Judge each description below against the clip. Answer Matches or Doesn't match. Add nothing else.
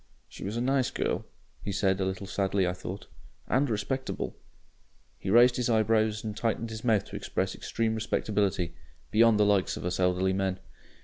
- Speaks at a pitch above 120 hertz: Doesn't match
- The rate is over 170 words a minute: Matches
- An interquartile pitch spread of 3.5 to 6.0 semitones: Doesn't match